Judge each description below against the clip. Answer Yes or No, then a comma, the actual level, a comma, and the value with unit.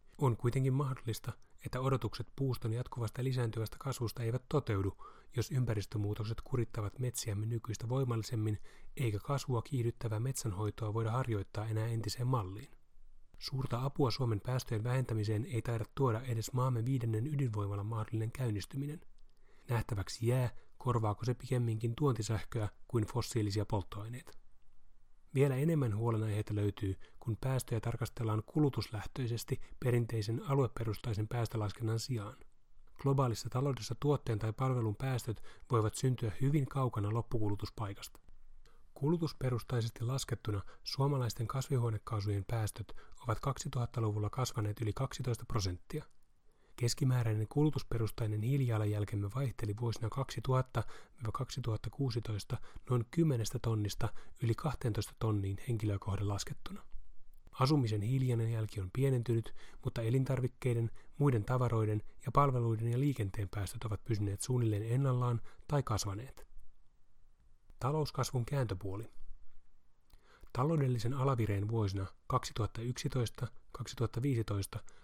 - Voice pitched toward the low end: Yes, low, 115 Hz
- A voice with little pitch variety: No, average, 3.3 semitones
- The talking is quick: No, average, 100 wpm